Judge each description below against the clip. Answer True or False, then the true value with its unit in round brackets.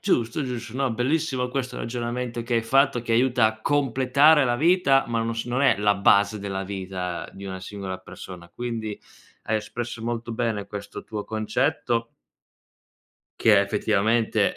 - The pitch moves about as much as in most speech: True (3.4 semitones)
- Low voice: True (115 Hz)